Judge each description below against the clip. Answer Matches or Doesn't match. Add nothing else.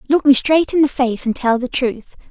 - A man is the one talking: Doesn't match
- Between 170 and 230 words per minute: Doesn't match